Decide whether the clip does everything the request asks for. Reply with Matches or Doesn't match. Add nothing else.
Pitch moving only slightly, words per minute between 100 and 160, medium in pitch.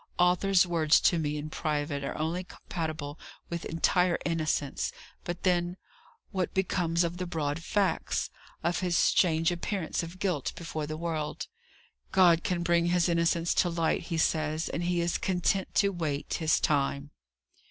Matches